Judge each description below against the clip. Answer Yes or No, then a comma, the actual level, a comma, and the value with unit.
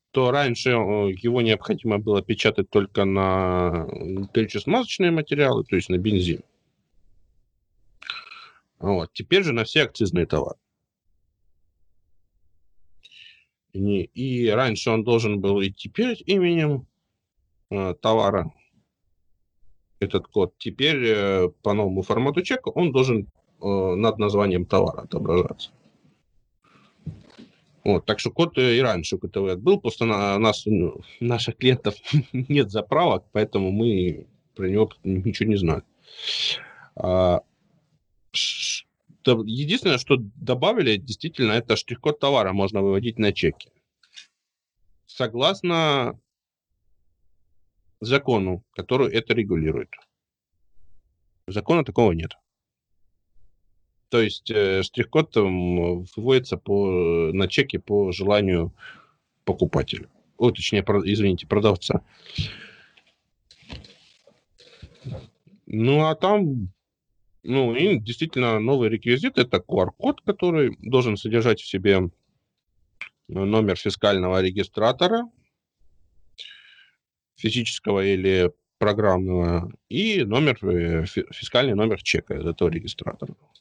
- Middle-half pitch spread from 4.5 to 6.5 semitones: Yes, average, 5.2 semitones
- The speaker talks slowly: Yes, slow, 95 wpm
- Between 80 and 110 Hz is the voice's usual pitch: Yes, low, 105 Hz